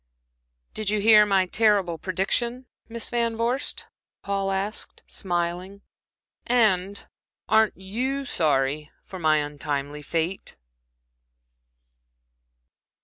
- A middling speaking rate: No, slow, 90 wpm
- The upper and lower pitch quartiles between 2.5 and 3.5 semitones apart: No, average, 4.4 semitones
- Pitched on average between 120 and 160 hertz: No, high, 195 Hz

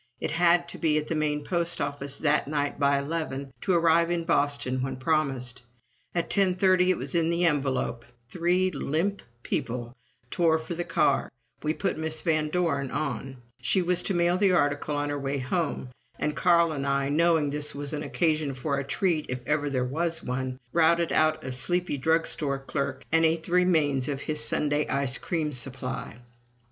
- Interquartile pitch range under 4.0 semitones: Yes, average, 3.4 semitones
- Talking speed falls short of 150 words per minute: No, average, 190 wpm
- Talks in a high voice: No, medium, 150 Hz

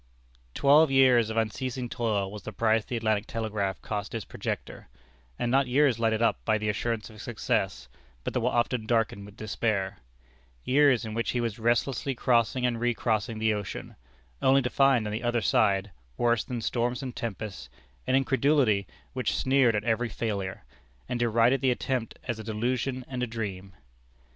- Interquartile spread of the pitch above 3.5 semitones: No, narrow, 2.6 semitones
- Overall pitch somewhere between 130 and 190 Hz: No, low, 115 Hz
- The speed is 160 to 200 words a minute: Yes, average, 170 wpm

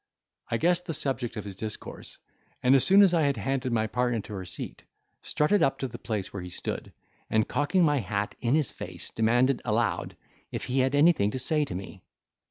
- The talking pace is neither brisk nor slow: No, fast, 210 wpm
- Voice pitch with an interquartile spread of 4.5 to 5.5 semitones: Yes, average, 4.9 semitones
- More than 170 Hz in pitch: No, low, 125 Hz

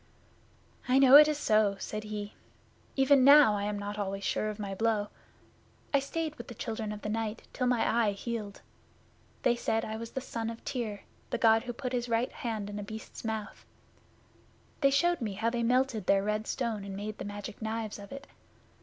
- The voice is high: Yes, high, 225 Hz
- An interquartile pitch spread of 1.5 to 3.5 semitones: Yes, average, 3.0 semitones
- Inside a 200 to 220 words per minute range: Yes, fast, 205 wpm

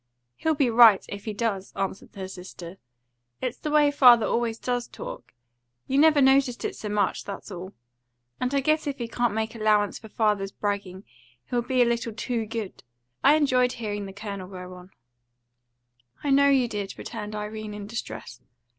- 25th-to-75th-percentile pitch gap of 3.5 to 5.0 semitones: Yes, average, 3.8 semitones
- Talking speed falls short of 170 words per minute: No, average, 180 wpm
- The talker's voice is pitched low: No, high, 220 Hz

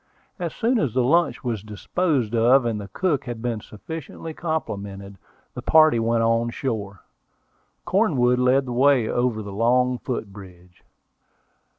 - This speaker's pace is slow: No, average, 150 wpm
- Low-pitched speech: Yes, low, 120 Hz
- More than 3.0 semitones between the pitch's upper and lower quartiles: Yes, average, 4.6 semitones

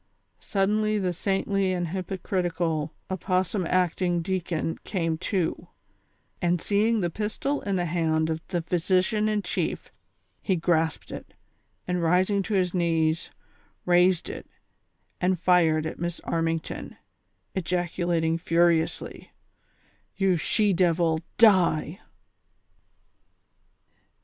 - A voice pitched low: No, medium, 180 Hz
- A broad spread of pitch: No, narrow, 2.6 semitones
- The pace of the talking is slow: Yes, slow, 110 wpm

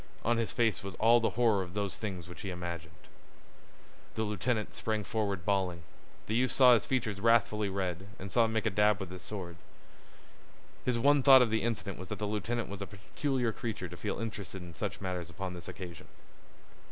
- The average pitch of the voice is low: Yes, low, 105 Hz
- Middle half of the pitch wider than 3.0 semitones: Yes, average, 3.6 semitones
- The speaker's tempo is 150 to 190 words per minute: No, average, 200 wpm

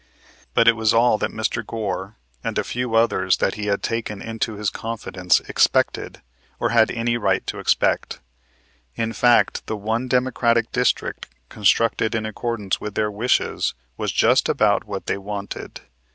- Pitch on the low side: Yes, low, 110 Hz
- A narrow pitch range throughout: Yes, narrow, 2.0 semitones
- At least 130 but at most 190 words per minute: Yes, average, 160 wpm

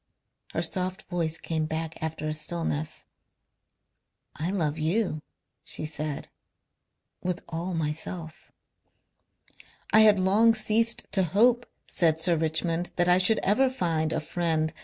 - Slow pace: Yes, slow, 130 wpm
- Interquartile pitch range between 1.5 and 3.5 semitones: Yes, average, 3.2 semitones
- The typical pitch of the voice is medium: Yes, medium, 170 Hz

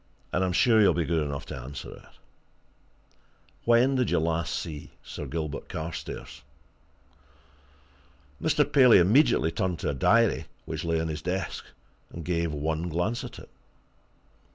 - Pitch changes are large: Yes, wide, 5.8 semitones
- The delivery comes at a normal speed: Yes, average, 150 wpm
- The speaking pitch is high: No, very low, 85 Hz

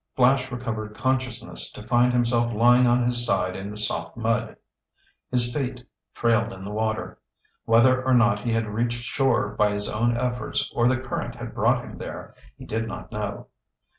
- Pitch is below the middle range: Yes, low, 120 Hz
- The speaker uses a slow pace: No, average, 180 wpm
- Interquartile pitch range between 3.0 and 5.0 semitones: No, narrow, 2.4 semitones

